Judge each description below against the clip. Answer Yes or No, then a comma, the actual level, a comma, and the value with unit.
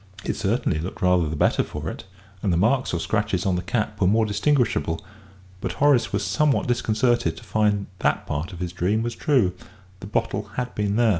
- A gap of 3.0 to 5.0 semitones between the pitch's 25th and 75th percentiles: Yes, average, 4.6 semitones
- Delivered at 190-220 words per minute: Yes, fast, 205 wpm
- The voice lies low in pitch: Yes, low, 105 Hz